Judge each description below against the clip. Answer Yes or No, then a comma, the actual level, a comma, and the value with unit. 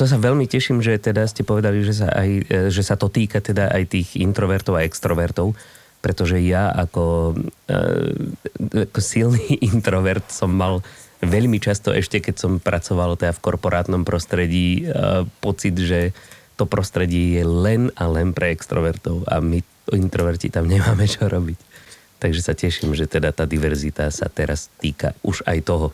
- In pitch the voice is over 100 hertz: No, very low, 95 Hz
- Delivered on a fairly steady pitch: No, average, 3.2 semitones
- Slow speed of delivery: No, average, 160 wpm